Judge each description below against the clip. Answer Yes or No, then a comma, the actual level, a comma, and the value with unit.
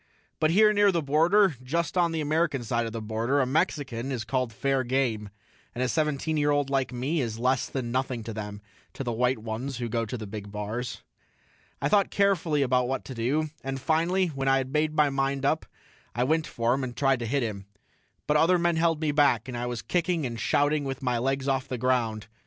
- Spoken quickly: Yes, fast, 225 wpm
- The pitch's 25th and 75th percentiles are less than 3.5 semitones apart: No, average, 4.2 semitones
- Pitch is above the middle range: No, low, 135 Hz